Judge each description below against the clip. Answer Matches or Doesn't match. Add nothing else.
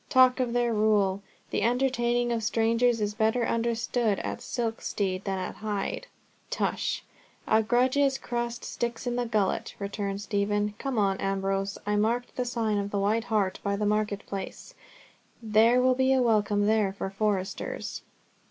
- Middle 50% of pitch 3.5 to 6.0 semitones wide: Doesn't match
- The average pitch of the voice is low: Doesn't match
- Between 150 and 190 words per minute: Matches